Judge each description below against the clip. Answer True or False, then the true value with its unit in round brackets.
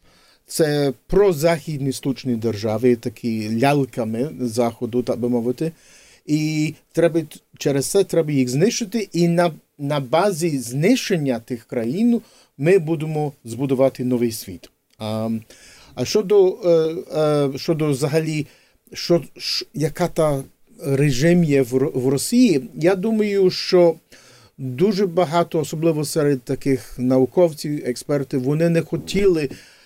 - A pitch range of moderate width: True (5.0 semitones)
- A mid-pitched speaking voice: True (150 Hz)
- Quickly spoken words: False (115 wpm)